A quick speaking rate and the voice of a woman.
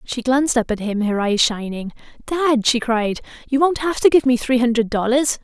Yes: fast, 220 wpm; female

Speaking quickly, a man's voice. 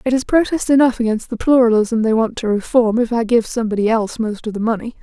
No: fast, 240 wpm; female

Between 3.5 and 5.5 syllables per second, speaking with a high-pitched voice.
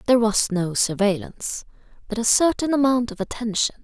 No: 5.7 syllables/s; high, 225 Hz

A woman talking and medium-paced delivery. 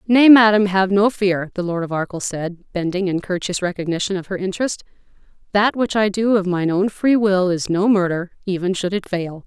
No: female; fast, 210 wpm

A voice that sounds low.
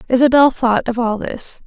No: high, 245 Hz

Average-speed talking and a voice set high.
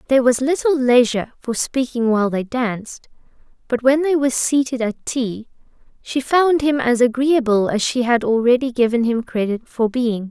Yes: average, 175 wpm; high, 245 Hz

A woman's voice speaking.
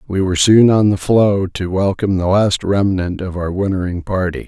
No: male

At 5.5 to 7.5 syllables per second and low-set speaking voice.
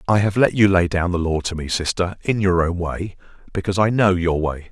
Yes: 5.7 syllables/s; very low, 90 Hz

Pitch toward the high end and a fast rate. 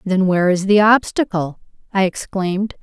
No: high, 195 Hz; average, 150 wpm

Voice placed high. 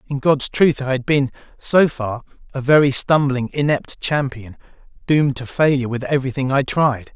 No: low, 135 Hz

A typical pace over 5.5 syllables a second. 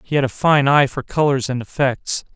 No: 5.1 syllables/s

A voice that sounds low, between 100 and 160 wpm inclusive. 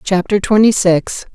No: high, 195 Hz; slow, 135 wpm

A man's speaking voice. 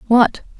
No: female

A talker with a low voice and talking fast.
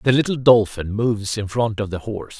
Yes: low, 110 Hz; fast, 225 wpm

